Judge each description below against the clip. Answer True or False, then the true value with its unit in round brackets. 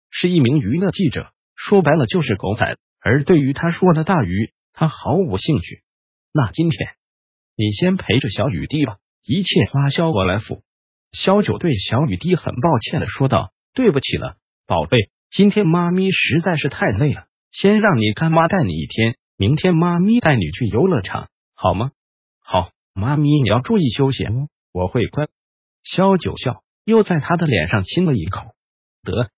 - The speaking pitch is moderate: True (145 Hz)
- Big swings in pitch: True (7.7 semitones)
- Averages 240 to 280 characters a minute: True (245 characters per minute)